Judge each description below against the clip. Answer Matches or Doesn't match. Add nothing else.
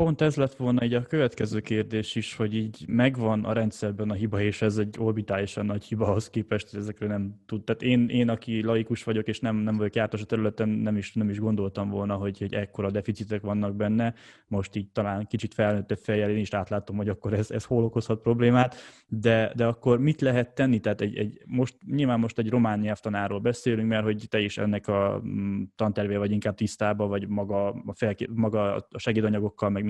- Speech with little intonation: Matches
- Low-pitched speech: Matches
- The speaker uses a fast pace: Matches